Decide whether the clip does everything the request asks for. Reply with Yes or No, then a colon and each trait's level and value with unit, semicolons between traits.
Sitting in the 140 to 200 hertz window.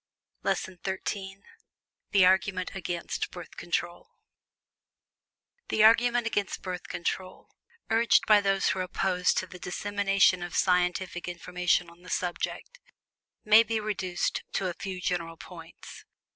Yes: medium, 185 Hz